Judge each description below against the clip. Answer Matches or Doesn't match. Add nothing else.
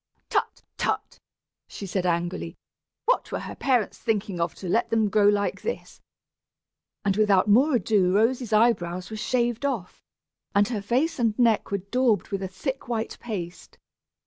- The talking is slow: Doesn't match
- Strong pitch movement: Doesn't match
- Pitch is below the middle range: Doesn't match